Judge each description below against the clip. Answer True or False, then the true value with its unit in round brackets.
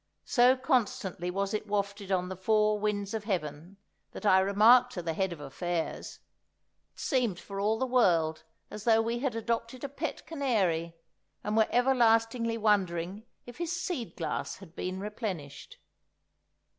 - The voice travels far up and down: False (4.2 semitones)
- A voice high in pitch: True (210 Hz)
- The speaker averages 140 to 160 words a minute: True (155 wpm)